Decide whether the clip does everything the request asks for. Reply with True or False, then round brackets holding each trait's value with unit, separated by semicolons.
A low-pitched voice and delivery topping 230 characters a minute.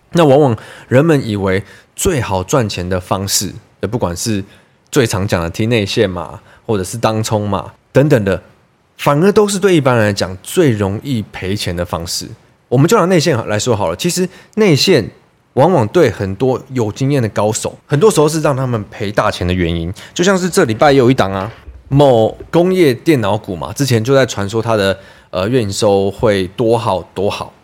True (110 Hz; 270 characters per minute)